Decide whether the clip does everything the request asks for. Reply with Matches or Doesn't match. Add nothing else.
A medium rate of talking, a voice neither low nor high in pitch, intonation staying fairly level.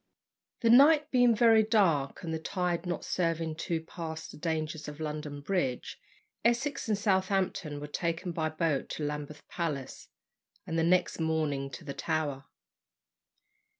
Doesn't match